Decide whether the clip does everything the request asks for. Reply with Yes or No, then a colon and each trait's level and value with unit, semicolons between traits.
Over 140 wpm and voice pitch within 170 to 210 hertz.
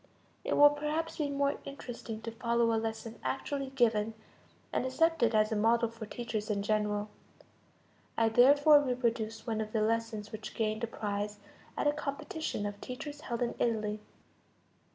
No: average, 160 wpm; high, 230 Hz